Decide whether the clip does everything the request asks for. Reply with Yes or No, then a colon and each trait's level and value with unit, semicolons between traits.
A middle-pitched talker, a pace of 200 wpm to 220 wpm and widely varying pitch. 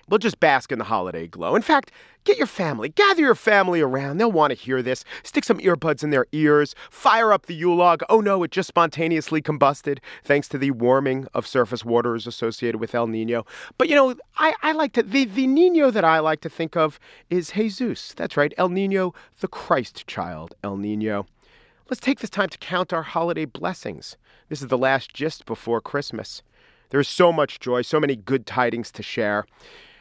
Yes: medium, 155 Hz; fast, 205 wpm; wide, 7.3 semitones